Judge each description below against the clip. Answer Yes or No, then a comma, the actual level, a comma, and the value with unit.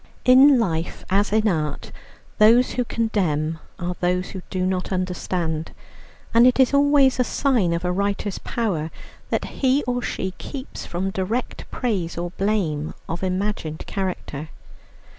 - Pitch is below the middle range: No, high, 190 Hz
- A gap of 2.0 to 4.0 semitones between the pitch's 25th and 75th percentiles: No, average, 5.3 semitones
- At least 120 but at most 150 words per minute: Yes, average, 145 wpm